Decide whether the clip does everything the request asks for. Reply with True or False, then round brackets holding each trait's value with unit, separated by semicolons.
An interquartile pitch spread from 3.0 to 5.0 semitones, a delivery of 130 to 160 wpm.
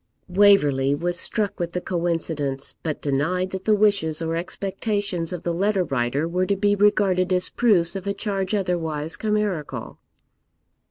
True (3.7 semitones; 155 wpm)